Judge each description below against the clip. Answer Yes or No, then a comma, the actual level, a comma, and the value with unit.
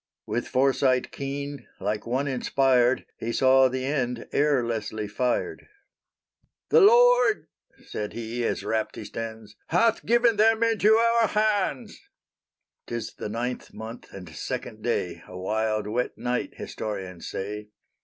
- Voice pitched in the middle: No, low, 125 Hz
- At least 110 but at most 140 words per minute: Yes, slow, 135 wpm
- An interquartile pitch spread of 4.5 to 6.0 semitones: Yes, wide, 5.6 semitones